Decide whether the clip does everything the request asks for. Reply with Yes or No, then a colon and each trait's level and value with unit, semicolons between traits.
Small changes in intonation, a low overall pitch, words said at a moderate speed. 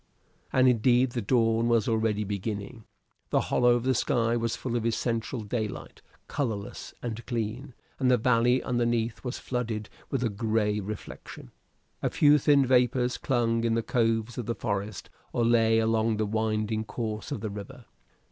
Yes: narrow, 2.1 semitones; low, 115 Hz; average, 165 wpm